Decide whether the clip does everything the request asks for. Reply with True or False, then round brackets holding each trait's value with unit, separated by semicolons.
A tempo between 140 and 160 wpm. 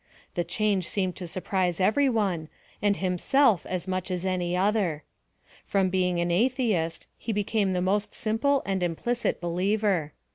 True (150 wpm)